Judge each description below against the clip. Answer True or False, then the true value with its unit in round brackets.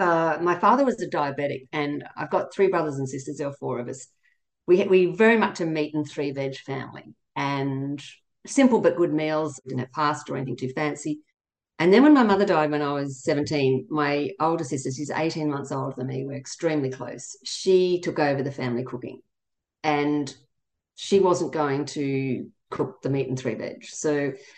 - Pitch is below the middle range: False (145 Hz)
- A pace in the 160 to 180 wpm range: False (200 wpm)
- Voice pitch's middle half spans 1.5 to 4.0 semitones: True (3.7 semitones)